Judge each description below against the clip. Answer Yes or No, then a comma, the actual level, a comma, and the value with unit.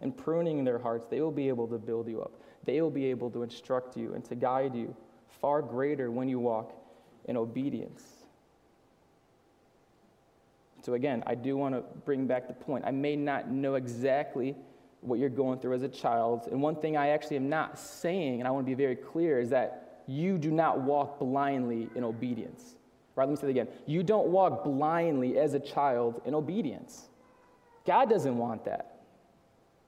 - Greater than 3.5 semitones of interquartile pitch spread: No, average, 3.0 semitones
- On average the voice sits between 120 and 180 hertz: Yes, low, 135 Hz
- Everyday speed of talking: Yes, average, 190 wpm